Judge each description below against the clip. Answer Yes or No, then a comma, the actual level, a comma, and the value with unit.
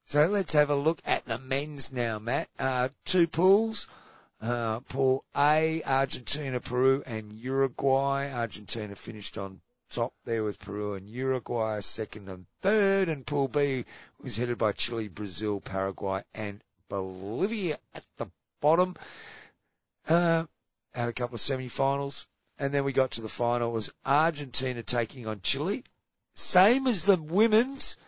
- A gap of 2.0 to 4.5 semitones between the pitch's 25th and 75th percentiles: No, average, 5.0 semitones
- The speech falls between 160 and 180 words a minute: No, average, 145 wpm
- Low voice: Yes, low, 130 Hz